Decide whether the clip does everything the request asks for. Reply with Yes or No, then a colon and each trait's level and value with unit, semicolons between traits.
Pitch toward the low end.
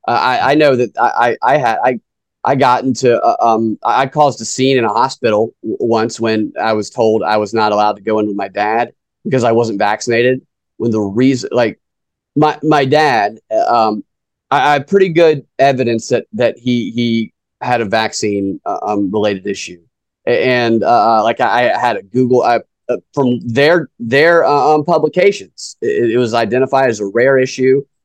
Yes: low, 120 Hz